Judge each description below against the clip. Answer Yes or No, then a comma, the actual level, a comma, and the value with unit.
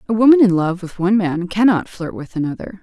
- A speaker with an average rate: No, fast, 235 wpm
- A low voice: No, high, 190 Hz